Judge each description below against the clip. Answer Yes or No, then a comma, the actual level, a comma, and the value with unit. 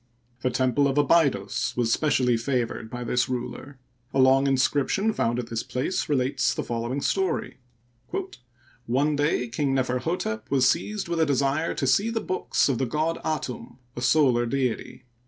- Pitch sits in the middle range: No, low, 130 Hz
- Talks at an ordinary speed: Yes, average, 165 wpm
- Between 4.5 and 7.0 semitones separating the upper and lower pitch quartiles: No, average, 3.2 semitones